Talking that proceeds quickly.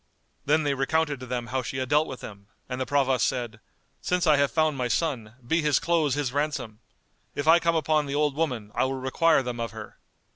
Yes: fast, 225 wpm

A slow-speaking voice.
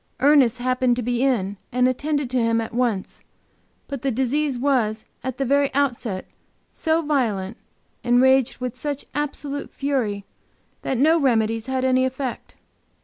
No: average, 150 wpm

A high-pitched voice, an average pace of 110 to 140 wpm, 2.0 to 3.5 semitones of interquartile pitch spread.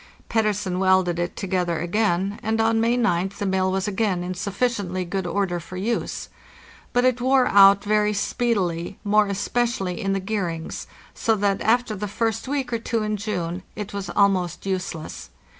No: high, 200 Hz; average, 170 wpm; average, 3.2 semitones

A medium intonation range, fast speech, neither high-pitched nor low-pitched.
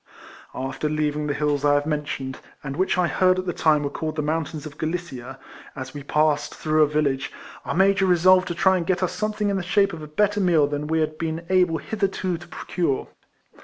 Yes: average, 3.7 semitones; fast, 220 wpm; medium, 160 Hz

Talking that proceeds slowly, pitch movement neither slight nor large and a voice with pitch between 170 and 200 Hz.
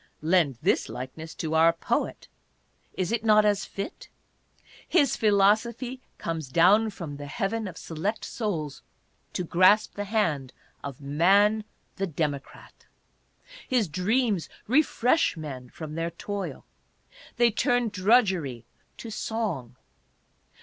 No: slow, 120 wpm; wide, 5.7 semitones; high, 190 Hz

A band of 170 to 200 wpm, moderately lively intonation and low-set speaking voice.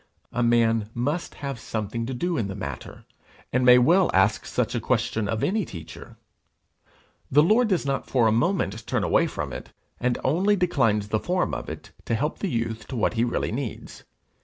No: average, 195 wpm; wide, 6.3 semitones; low, 120 Hz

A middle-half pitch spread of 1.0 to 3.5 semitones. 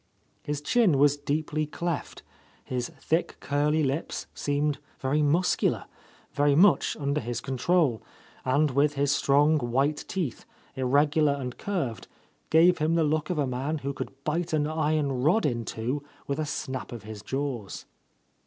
Yes: narrow, 2.6 semitones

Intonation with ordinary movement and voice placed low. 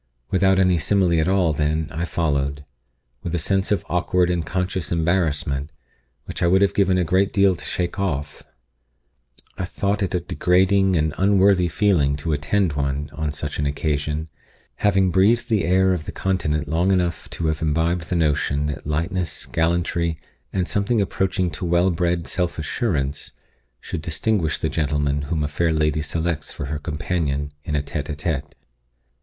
Yes: average, 3.8 semitones; very low, 85 Hz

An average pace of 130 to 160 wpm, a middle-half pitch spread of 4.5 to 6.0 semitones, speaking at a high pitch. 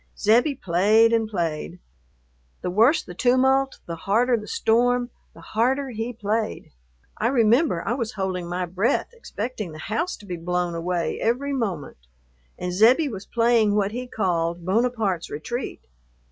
Yes: average, 150 wpm; average, 5.2 semitones; high, 220 Hz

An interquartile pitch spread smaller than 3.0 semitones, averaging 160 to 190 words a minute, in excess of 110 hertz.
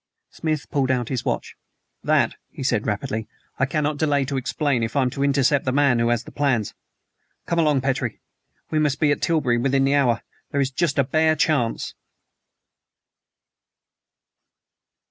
Yes: narrow, 2.6 semitones; average, 165 wpm; low, 135 Hz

